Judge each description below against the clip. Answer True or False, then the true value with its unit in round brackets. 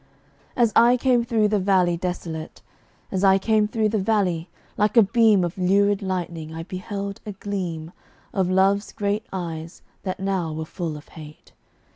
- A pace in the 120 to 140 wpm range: False (165 wpm)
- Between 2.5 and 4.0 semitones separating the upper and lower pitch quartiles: True (3.2 semitones)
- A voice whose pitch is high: True (195 Hz)